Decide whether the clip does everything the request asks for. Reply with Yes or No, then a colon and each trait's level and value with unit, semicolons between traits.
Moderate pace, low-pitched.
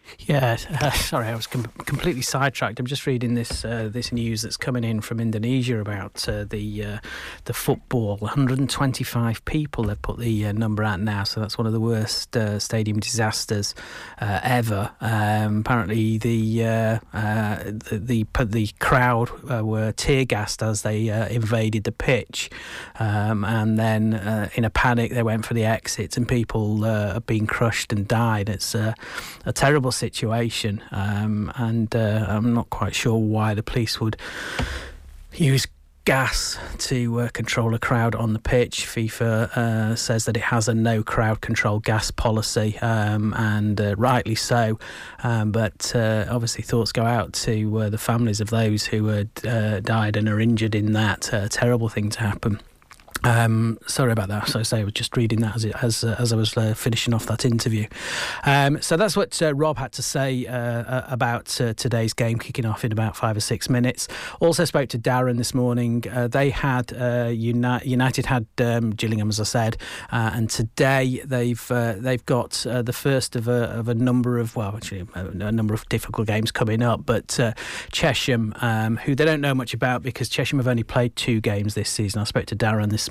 Yes: average, 195 wpm; low, 115 Hz